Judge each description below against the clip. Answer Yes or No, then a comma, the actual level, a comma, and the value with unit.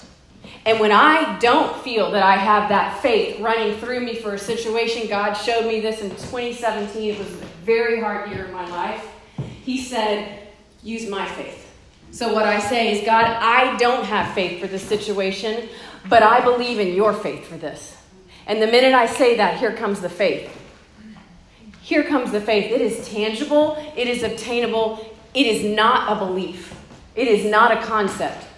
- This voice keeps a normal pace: Yes, average, 185 wpm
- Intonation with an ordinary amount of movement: No, narrow, 2.3 semitones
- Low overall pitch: No, high, 220 Hz